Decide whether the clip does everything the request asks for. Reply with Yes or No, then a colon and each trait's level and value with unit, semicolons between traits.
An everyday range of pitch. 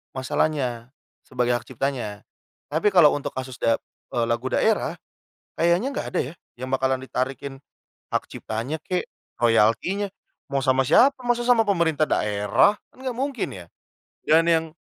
No: wide, 6.5 semitones